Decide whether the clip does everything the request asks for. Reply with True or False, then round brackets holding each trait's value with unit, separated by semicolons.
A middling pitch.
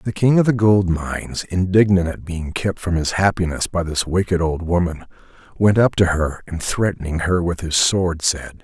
False (90 Hz)